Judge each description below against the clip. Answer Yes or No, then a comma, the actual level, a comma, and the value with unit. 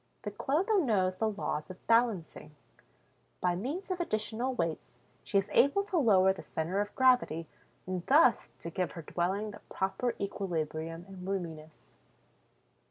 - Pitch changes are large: Yes, wide, 5.8 semitones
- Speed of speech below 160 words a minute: Yes, average, 150 wpm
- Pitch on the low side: No, high, 195 Hz